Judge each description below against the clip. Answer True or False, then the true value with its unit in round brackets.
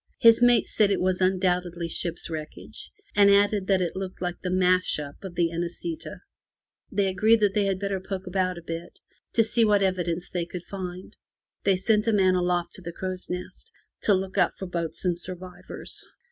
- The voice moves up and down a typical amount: False (2.0 semitones)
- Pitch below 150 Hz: False (185 Hz)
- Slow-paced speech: False (200 wpm)